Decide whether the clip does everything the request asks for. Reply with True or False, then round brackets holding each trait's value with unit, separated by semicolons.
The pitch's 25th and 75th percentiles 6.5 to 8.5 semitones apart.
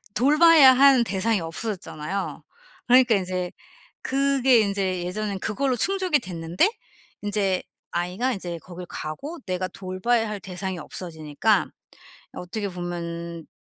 False (5.6 semitones)